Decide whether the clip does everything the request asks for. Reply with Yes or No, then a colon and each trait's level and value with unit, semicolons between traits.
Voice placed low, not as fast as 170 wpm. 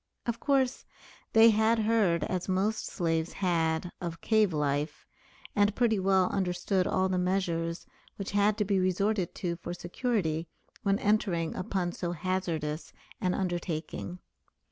No: medium, 185 Hz; average, 140 wpm